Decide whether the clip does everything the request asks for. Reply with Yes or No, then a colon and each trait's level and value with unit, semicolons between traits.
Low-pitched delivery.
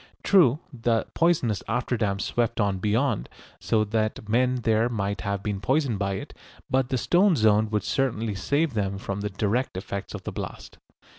Yes: low, 110 Hz